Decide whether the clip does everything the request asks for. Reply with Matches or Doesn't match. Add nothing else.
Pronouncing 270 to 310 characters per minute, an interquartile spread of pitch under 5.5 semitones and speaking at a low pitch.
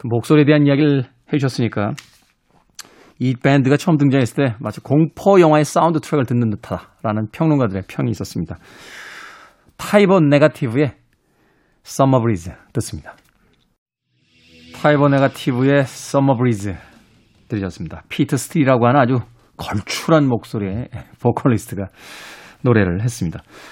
Doesn't match